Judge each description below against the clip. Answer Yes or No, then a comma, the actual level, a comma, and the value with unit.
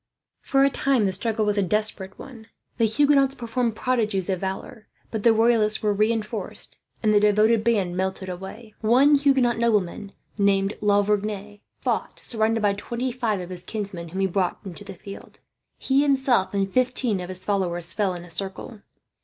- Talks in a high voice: Yes, high, 210 Hz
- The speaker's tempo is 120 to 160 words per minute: No, average, 180 wpm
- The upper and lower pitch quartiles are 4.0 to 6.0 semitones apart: No, average, 3.4 semitones